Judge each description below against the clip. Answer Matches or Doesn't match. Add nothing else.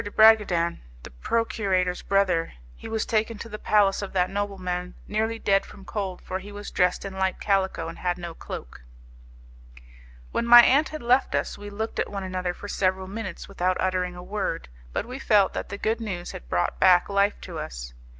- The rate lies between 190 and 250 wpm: Matches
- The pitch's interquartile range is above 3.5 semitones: Doesn't match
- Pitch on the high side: Matches